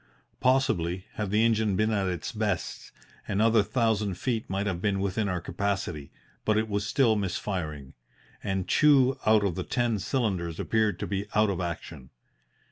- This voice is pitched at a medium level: No, low, 100 Hz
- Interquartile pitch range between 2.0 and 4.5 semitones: Yes, average, 3.2 semitones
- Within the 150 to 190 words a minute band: Yes, average, 165 wpm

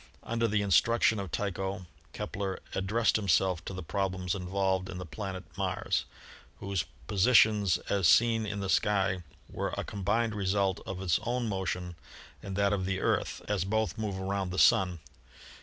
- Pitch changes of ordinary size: No, narrow, 1.9 semitones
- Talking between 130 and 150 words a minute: No, average, 165 wpm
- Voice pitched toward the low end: Yes, very low, 95 Hz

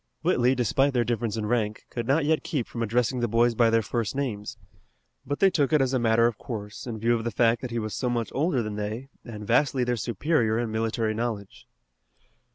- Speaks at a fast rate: Yes, fast, 225 wpm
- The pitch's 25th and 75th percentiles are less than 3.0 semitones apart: Yes, narrow, 2.4 semitones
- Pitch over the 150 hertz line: No, low, 120 Hz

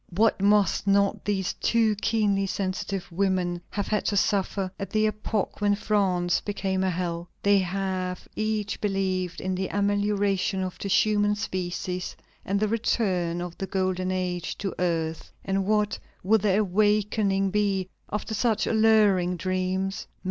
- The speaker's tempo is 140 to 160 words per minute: Yes, average, 150 wpm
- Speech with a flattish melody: Yes, narrow, 2.0 semitones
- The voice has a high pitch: Yes, high, 195 Hz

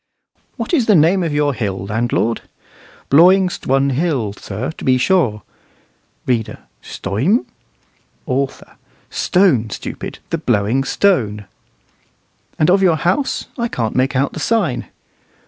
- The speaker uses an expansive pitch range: Yes, wide, 7.8 semitones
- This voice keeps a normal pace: No, slow, 130 wpm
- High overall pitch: No, low, 135 Hz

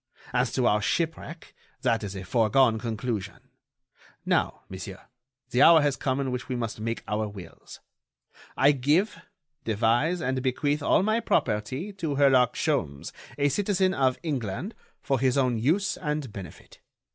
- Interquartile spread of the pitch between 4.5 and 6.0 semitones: Yes, average, 5.0 semitones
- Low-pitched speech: Yes, low, 130 Hz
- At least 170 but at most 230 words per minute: No, average, 150 wpm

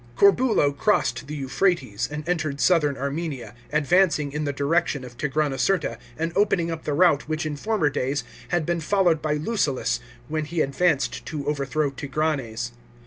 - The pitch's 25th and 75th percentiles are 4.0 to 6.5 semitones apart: No, average, 3.3 semitones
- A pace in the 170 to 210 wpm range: No, average, 155 wpm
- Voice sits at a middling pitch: Yes, medium, 150 Hz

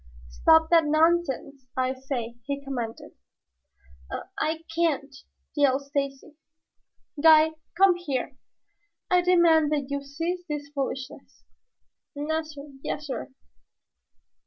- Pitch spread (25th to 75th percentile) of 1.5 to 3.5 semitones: Yes, average, 2.8 semitones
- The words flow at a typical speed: No, slow, 100 wpm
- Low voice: No, very high, 290 Hz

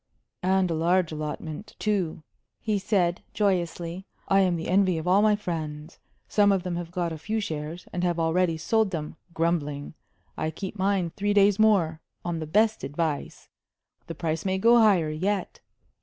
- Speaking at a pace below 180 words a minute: Yes, average, 170 wpm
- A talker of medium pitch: Yes, medium, 180 Hz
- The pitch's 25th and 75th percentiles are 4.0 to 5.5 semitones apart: No, average, 3.6 semitones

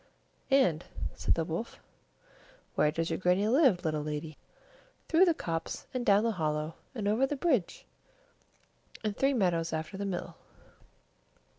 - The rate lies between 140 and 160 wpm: Yes, average, 150 wpm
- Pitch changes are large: Yes, wide, 6.8 semitones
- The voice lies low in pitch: No, medium, 185 Hz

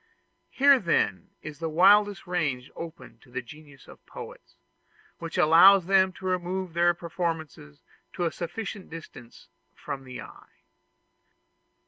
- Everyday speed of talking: No, slow, 130 wpm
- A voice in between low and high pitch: Yes, medium, 170 Hz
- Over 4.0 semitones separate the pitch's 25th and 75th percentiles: No, average, 3.6 semitones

